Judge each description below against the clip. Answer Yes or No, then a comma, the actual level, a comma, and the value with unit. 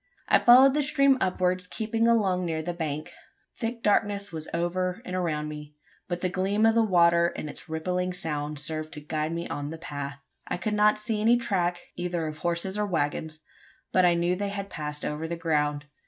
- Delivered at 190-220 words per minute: Yes, average, 200 wpm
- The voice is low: No, medium, 175 Hz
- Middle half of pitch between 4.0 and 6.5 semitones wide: Yes, average, 4.5 semitones